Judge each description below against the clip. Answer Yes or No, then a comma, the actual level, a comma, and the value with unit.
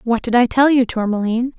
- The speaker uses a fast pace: Yes, fast, 225 wpm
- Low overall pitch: No, high, 240 Hz